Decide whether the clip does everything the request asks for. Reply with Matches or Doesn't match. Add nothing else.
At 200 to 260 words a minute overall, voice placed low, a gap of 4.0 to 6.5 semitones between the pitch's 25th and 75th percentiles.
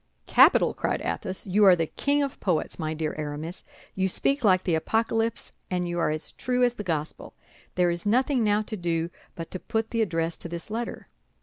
Doesn't match